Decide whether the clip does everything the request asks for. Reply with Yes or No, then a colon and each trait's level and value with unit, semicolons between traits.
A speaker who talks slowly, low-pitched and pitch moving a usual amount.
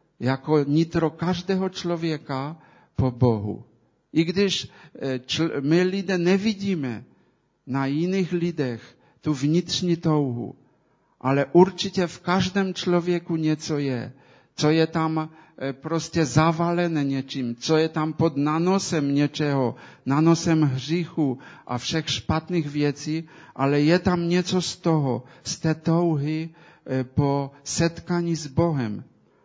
No: slow, 110 wpm; medium, 155 Hz; average, 3.8 semitones